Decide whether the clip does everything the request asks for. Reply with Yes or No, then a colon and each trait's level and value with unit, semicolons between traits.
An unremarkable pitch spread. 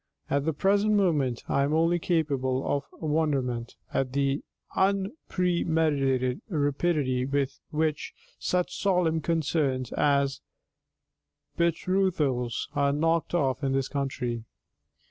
Yes: average, 3.9 semitones